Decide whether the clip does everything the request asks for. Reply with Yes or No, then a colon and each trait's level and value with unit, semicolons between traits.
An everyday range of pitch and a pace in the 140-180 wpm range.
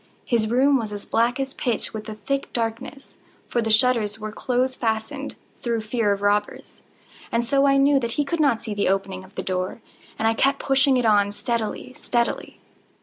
No: average, 3.6 semitones; average, 200 wpm